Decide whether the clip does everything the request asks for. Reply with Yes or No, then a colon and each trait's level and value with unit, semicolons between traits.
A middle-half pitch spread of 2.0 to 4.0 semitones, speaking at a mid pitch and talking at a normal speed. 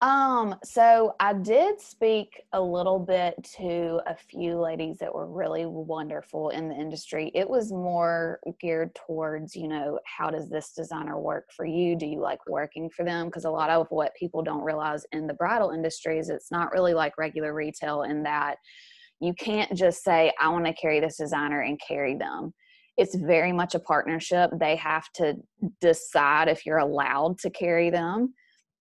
Yes: average, 2.7 semitones; medium, 165 Hz; average, 185 wpm